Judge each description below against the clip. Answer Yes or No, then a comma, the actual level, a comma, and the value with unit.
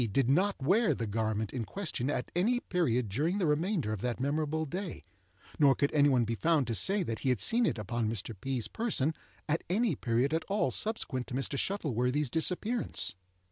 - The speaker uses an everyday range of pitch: No, wide, 7.0 semitones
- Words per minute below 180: No, average, 195 wpm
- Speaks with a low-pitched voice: No, medium, 145 Hz